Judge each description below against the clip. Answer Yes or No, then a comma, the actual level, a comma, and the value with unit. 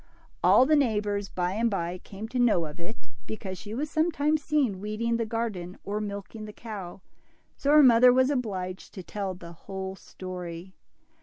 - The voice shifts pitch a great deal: No, average, 4.5 semitones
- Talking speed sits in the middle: Yes, average, 175 wpm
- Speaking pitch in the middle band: No, high, 210 Hz